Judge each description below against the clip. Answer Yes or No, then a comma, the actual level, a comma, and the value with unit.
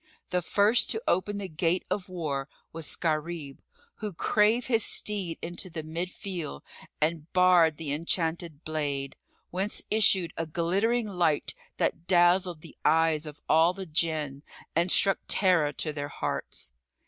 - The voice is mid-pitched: Yes, medium, 170 Hz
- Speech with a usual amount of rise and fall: Yes, average, 3.1 semitones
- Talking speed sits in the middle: Yes, average, 150 wpm